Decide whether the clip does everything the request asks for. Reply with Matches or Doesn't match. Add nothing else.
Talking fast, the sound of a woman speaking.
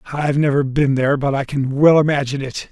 Doesn't match